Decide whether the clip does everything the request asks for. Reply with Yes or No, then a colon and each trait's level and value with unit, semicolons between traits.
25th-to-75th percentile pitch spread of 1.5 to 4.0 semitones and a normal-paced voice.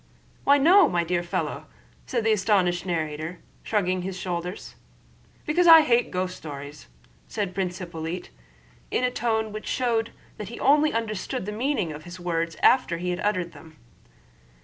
No: average, 4.9 semitones; average, 160 wpm